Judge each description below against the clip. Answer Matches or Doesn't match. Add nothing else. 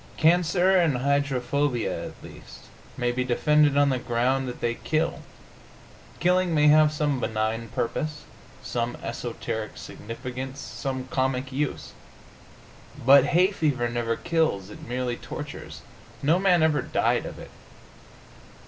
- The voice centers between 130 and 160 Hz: Matches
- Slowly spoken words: Matches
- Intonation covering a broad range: Doesn't match